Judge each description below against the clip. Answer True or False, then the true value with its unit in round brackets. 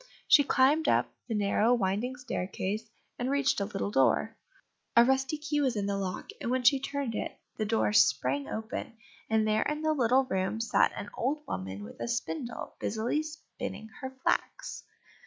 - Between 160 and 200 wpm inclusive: True (175 wpm)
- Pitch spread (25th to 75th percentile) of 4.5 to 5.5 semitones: True (4.8 semitones)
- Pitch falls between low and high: False (230 Hz)